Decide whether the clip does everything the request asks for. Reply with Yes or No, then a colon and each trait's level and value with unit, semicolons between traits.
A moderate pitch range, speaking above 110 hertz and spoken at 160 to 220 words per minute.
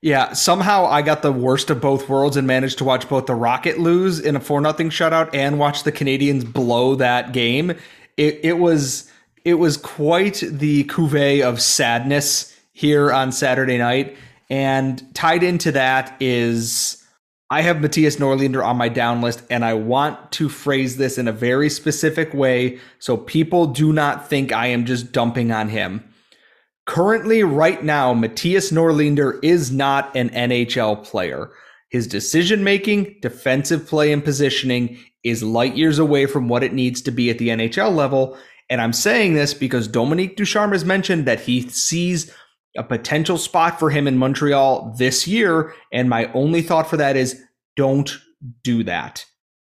Yes: average, 4.1 semitones; medium, 140 Hz; average, 170 wpm